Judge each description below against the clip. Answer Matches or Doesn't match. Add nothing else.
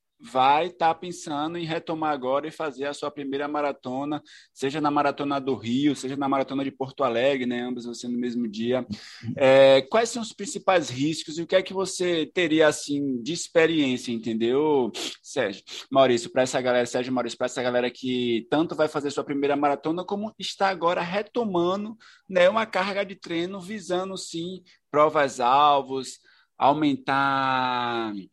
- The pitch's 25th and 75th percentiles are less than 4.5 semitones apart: Doesn't match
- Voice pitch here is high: Doesn't match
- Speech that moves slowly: Doesn't match